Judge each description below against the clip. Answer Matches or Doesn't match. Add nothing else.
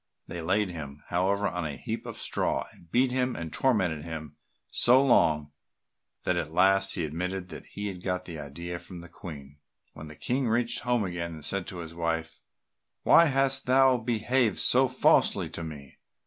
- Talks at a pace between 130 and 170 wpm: Doesn't match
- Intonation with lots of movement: Matches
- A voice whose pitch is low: Matches